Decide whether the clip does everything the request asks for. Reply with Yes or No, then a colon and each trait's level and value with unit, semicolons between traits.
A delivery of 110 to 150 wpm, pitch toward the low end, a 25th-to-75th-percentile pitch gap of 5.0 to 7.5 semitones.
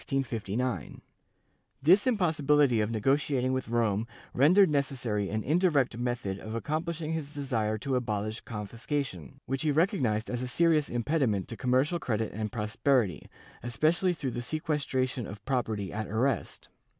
Yes: average, 140 wpm; low, 125 Hz; average, 5.3 semitones